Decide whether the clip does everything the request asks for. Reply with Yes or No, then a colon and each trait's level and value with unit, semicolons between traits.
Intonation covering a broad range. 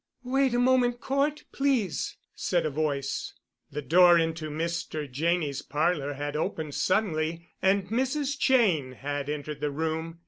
Yes: wide, 7.7 semitones